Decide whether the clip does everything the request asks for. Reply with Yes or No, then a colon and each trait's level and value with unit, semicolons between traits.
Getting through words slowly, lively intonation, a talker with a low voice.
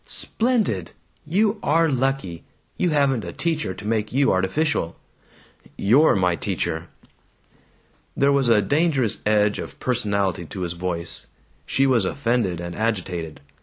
Yes: slow, 130 wpm; wide, 7.3 semitones; low, 110 Hz